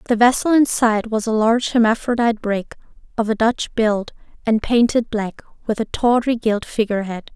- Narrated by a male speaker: No, female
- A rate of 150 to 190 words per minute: Yes, average, 180 wpm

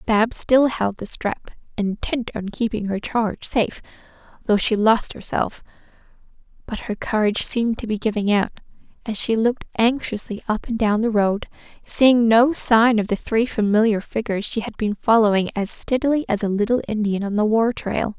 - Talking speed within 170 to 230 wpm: Yes, average, 180 wpm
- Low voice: No, high, 220 Hz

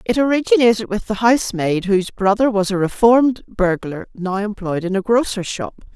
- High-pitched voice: Yes, high, 210 Hz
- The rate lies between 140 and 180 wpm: Yes, average, 170 wpm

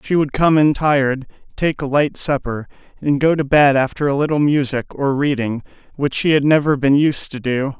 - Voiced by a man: Yes, male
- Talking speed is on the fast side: Yes, fast, 210 wpm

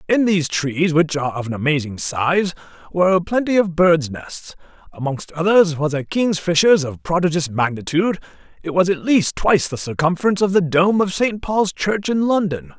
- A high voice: No, medium, 170 Hz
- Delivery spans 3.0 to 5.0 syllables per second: No, 5.2 syllables/s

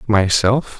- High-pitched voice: No, low, 110 Hz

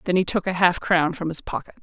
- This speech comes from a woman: Yes, female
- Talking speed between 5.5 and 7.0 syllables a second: Yes, 6.1 syllables/s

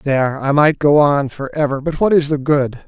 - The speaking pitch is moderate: Yes, medium, 145 Hz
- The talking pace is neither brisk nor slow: No, fast, 250 wpm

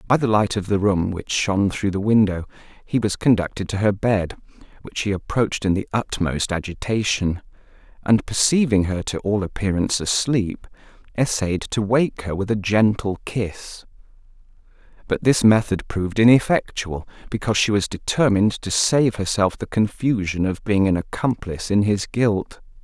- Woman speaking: No, male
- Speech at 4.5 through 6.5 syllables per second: Yes, 4.9 syllables/s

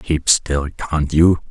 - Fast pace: No, average, 160 wpm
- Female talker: No, male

